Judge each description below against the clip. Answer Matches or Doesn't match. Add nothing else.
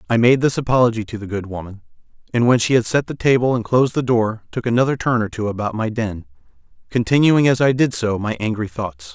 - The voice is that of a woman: Doesn't match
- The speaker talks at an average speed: Doesn't match